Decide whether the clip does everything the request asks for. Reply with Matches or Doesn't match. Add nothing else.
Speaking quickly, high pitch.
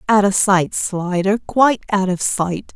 Doesn't match